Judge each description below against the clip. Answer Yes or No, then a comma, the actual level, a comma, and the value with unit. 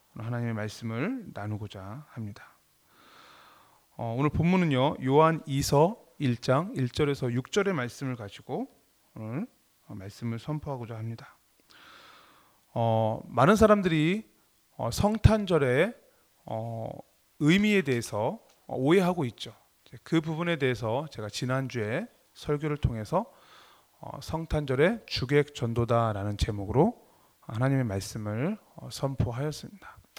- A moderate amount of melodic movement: No, wide, 5.8 semitones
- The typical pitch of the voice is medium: No, low, 130 Hz